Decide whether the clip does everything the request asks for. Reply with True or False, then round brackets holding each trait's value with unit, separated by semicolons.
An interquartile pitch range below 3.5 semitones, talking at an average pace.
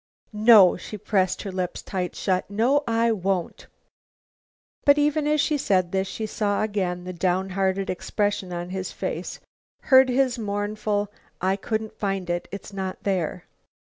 True (2.8 semitones; 150 wpm)